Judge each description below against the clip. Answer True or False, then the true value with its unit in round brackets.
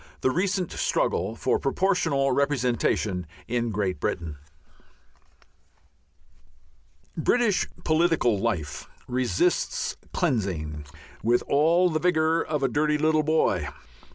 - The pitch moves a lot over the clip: True (6.8 semitones)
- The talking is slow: True (100 wpm)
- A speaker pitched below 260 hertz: True (140 Hz)